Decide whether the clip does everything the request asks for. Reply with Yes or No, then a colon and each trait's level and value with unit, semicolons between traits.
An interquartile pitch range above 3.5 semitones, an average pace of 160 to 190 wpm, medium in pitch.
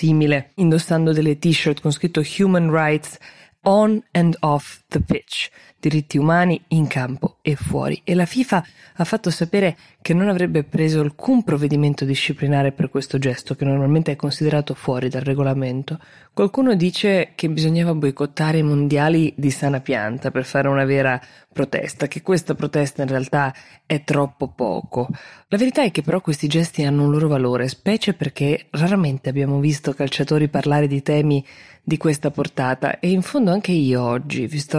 No: average, 3.2 semitones; average, 165 wpm; medium, 150 Hz